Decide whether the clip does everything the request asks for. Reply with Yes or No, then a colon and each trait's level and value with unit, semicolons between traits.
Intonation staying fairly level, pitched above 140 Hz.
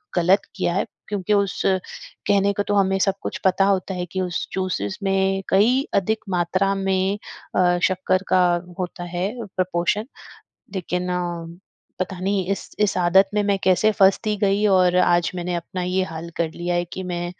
Yes: narrow, 1.6 semitones; high, 190 Hz